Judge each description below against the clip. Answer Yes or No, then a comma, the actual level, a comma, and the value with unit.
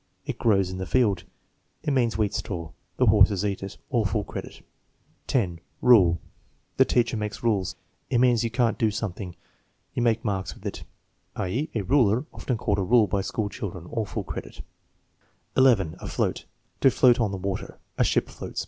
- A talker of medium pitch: No, low, 105 Hz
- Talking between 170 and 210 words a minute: Yes, average, 180 wpm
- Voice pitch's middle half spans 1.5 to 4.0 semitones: Yes, average, 3.6 semitones